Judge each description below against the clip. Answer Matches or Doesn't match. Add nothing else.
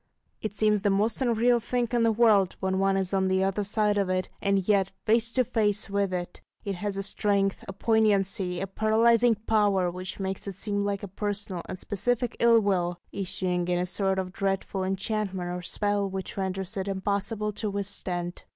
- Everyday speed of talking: Matches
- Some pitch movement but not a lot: Doesn't match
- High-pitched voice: Matches